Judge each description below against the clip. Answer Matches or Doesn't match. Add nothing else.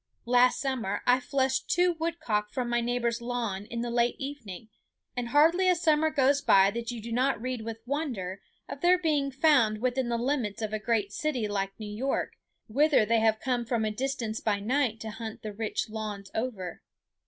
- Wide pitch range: Doesn't match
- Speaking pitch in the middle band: Doesn't match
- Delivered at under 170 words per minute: Doesn't match